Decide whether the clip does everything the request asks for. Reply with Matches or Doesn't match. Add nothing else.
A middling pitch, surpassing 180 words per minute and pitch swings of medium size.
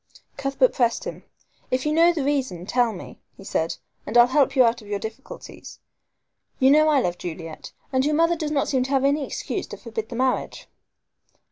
Doesn't match